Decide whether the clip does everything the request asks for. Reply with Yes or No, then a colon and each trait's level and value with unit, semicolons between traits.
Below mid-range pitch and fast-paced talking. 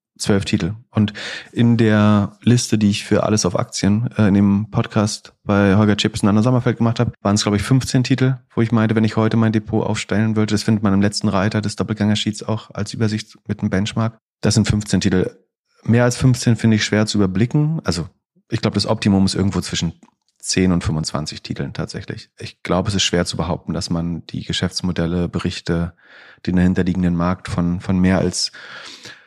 Yes: low, 105 Hz; fast, 200 wpm